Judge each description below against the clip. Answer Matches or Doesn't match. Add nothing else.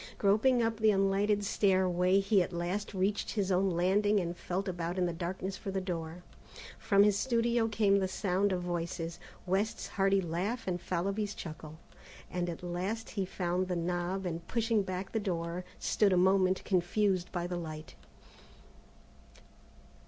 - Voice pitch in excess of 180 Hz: Matches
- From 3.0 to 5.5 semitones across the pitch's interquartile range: Doesn't match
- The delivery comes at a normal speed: Matches